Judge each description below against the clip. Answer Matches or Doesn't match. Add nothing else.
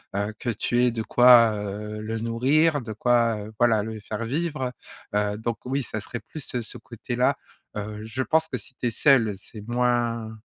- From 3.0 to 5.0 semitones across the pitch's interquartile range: Doesn't match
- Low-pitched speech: Matches